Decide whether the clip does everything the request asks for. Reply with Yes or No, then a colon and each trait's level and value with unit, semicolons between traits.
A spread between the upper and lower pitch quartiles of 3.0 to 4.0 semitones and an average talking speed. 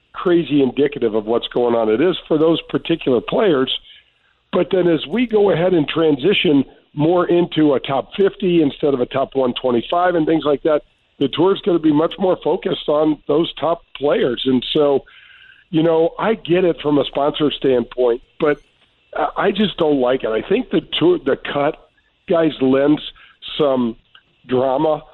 No: average, 4.6 semitones; average, 180 wpm